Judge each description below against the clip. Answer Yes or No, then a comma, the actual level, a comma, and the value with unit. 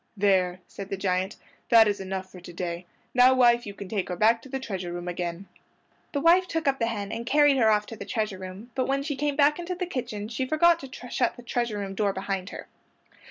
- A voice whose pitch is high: Yes, high, 220 Hz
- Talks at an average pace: No, fast, 245 wpm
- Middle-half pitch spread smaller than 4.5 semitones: No, wide, 5.6 semitones